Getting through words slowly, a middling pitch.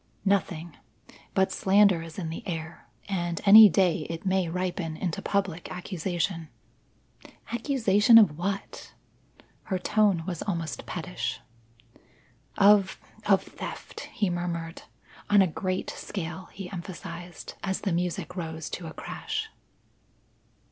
Yes: slow, 120 wpm; medium, 180 Hz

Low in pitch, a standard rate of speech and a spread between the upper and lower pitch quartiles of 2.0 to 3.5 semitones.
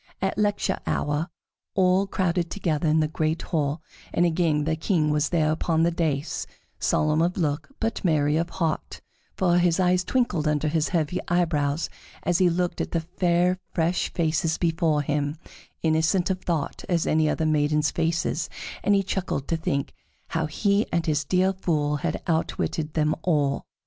No: medium, 165 Hz; average, 170 wpm; average, 2.7 semitones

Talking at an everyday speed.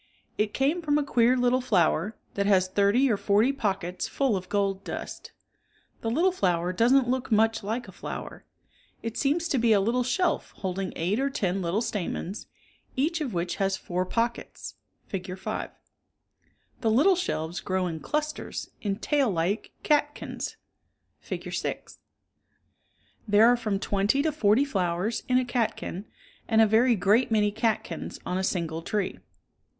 Yes: average, 160 wpm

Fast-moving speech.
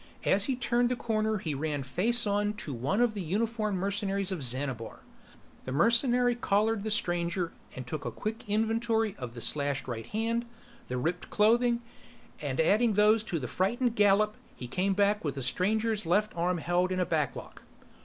No: average, 180 wpm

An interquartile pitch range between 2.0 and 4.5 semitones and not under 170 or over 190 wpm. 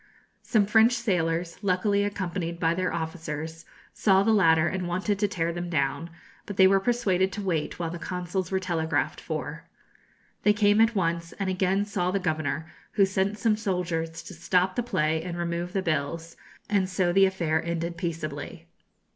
Yes: average, 3.0 semitones; average, 175 wpm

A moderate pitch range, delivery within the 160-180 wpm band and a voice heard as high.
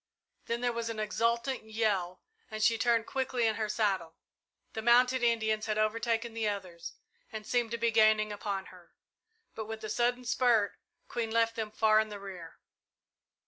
No: narrow, 1.6 semitones; average, 175 wpm; high, 220 Hz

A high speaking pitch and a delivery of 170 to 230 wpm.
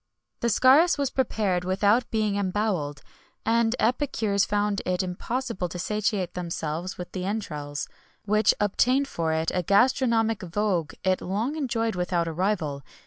No: high, 200 Hz; average, 145 wpm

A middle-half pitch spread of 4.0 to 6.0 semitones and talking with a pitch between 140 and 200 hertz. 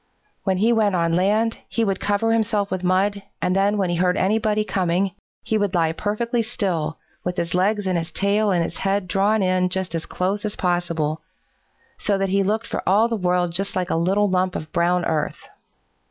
No: narrow, 2.6 semitones; high, 190 Hz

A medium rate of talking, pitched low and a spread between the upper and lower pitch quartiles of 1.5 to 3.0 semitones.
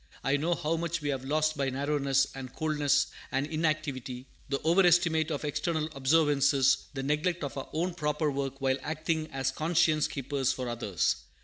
No: average, 170 wpm; medium, 145 Hz; average, 2.7 semitones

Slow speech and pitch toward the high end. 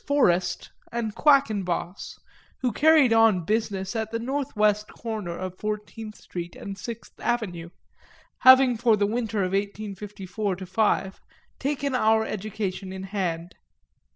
Yes: slow, 125 wpm; high, 210 Hz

